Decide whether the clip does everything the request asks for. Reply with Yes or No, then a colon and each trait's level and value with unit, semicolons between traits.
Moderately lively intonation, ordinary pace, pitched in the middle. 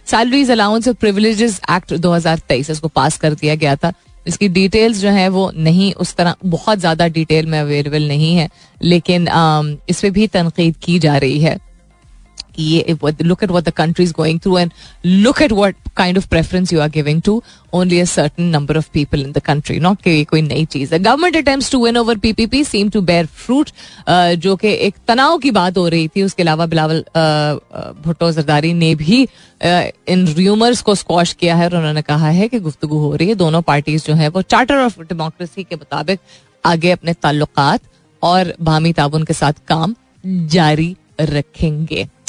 Yes: average, 3.6 semitones; average, 175 wpm; medium, 170 Hz